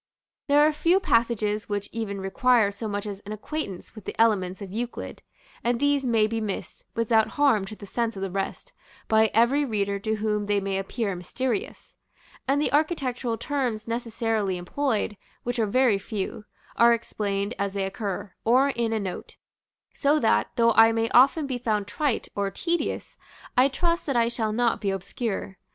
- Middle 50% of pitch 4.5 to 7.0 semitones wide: No, average, 3.7 semitones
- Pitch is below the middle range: No, high, 225 Hz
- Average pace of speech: Yes, average, 180 wpm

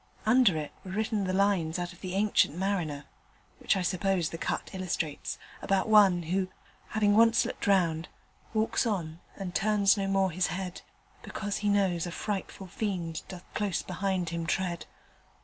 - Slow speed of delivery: No, average, 165 wpm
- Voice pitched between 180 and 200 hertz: Yes, high, 190 Hz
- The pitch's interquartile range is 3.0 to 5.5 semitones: No, narrow, 2.6 semitones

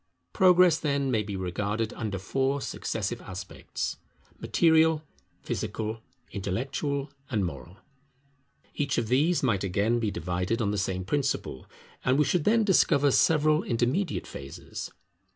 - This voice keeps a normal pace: No, slow, 130 wpm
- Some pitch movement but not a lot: No, wide, 6.7 semitones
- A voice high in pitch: No, low, 120 Hz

